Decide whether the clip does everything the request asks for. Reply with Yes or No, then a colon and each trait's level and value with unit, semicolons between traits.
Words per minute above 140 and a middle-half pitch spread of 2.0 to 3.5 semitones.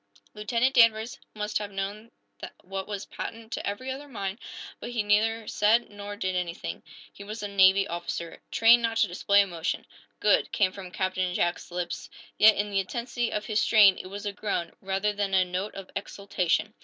Yes: average, 185 wpm; narrow, 2.5 semitones